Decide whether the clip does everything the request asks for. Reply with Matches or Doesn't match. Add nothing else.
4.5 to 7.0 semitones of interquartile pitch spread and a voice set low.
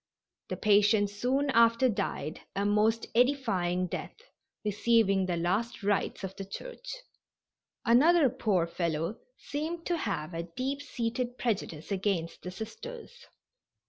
Doesn't match